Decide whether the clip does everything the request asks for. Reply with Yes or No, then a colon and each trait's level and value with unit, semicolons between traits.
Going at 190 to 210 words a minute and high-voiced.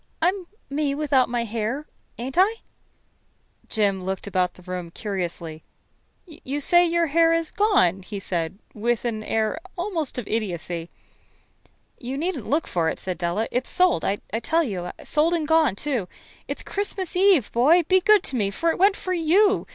No: average, 170 wpm; very high, 265 Hz